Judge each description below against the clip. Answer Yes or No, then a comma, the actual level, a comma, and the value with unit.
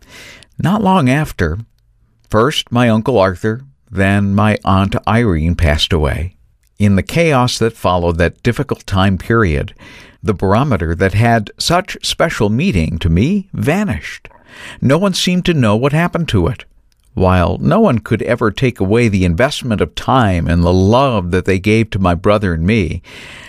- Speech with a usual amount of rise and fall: Yes, average, 4.7 semitones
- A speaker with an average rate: Yes, average, 160 wpm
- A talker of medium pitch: No, low, 105 Hz